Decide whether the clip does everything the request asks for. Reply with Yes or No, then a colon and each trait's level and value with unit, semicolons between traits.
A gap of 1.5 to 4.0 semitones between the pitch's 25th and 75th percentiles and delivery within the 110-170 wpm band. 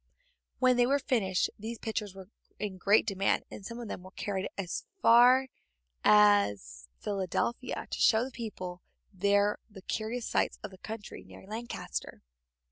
Yes: average, 3.5 semitones; average, 155 wpm